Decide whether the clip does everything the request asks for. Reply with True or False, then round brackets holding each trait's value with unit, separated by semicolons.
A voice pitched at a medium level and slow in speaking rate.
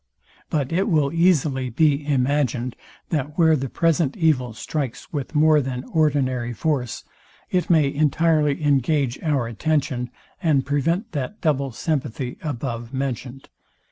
True (145 Hz; 130 wpm)